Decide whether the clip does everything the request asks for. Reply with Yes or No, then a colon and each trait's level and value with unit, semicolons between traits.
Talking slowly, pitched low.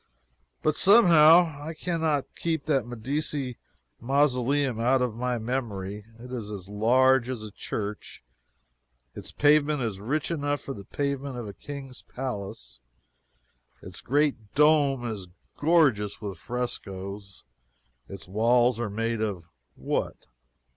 Yes: slow, 130 wpm; low, 125 Hz